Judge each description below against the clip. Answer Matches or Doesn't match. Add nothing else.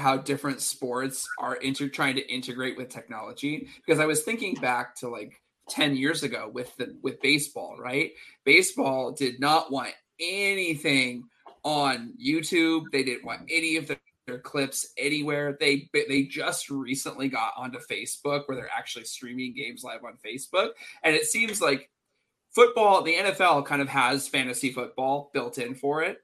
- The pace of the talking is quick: Doesn't match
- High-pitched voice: Doesn't match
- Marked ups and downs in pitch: Doesn't match